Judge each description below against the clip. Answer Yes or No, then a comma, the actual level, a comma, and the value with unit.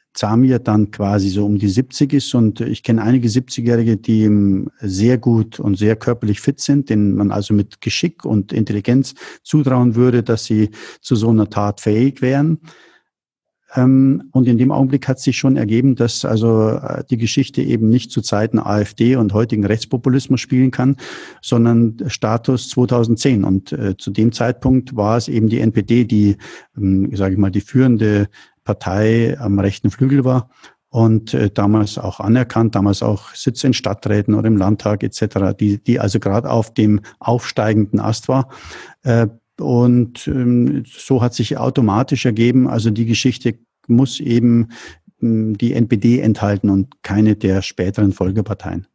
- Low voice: Yes, low, 115 Hz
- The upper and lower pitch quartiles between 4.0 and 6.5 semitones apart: No, average, 3.4 semitones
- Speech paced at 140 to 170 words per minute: Yes, average, 155 wpm